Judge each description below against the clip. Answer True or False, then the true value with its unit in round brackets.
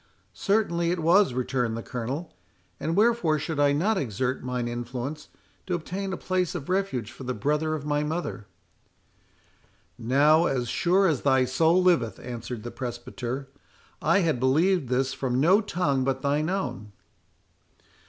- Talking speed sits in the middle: True (150 wpm)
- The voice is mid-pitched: True (145 Hz)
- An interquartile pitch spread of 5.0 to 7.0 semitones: True (5.6 semitones)